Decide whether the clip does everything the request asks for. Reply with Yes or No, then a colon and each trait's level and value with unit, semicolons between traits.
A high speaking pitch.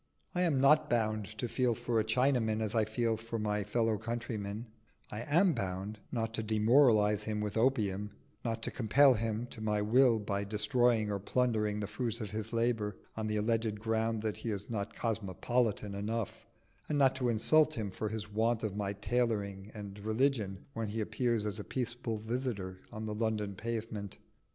No: low, 110 Hz